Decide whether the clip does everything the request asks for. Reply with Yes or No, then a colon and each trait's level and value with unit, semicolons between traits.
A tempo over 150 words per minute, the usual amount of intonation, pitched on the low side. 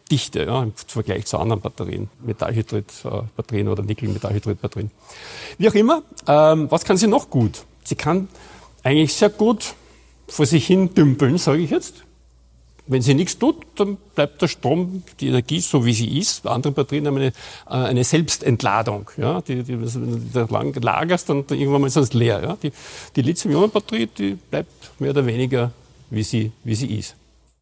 No: average, 175 wpm; wide, 5.9 semitones; low, 130 Hz